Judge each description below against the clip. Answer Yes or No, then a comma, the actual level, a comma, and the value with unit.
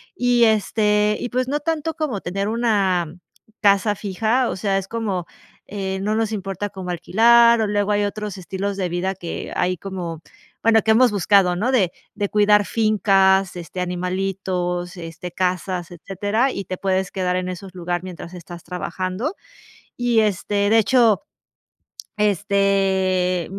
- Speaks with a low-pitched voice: No, high, 195 Hz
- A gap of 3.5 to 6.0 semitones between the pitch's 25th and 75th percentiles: No, average, 2.8 semitones